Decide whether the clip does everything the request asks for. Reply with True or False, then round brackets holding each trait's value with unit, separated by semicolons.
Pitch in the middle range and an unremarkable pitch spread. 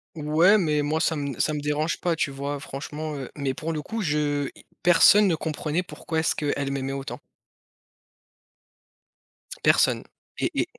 False (150 Hz; 2.3 semitones)